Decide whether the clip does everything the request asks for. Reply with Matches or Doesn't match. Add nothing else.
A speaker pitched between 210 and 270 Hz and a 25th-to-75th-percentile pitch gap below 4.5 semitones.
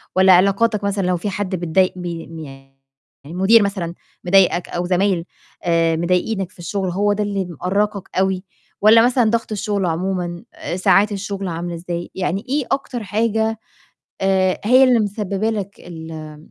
Doesn't match